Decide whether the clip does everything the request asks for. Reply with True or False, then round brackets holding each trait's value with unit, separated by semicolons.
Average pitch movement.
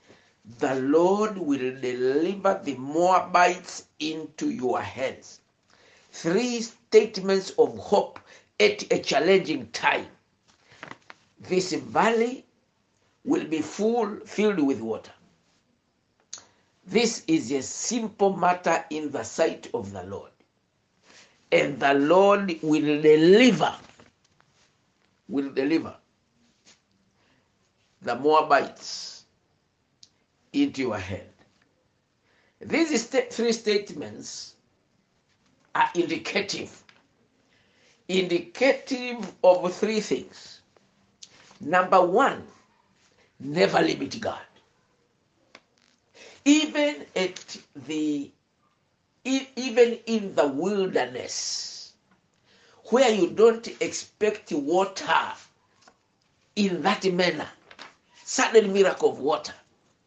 False (6.2 semitones)